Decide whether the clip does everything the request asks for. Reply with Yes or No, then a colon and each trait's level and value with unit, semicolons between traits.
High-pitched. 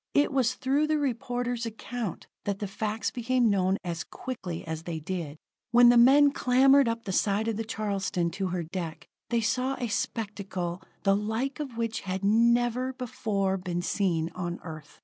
Yes: high, 215 Hz